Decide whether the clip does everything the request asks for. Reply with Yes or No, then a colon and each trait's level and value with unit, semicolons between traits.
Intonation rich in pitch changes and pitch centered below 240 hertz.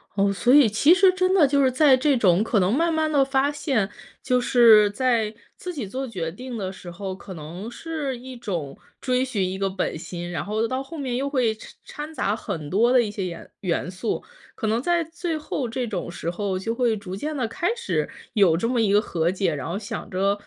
Yes: wide, 5.9 semitones; high, 230 Hz